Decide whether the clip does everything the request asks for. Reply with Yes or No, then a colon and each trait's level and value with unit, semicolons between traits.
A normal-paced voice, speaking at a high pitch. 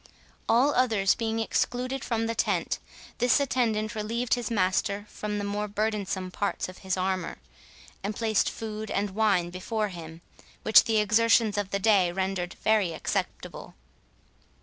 Yes: average, 150 wpm; high, 210 Hz